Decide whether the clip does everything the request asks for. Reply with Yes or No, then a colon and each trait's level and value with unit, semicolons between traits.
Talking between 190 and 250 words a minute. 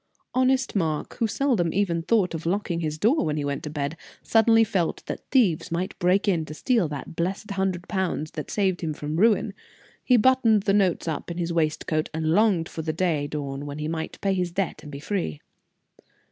Yes: fast, 205 wpm